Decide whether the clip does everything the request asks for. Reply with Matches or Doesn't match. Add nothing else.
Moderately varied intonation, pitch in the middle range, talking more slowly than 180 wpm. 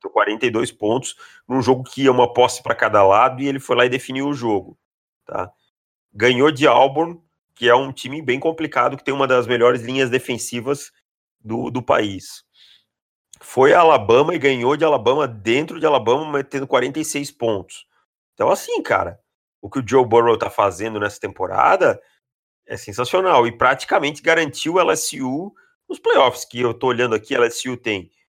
Doesn't match